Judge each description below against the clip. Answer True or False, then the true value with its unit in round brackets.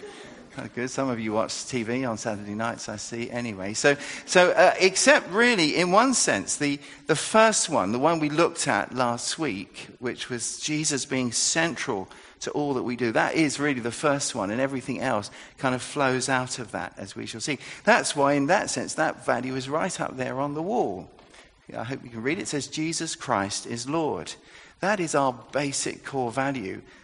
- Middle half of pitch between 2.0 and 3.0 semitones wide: False (4.4 semitones)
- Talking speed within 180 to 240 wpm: True (205 wpm)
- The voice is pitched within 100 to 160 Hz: True (135 Hz)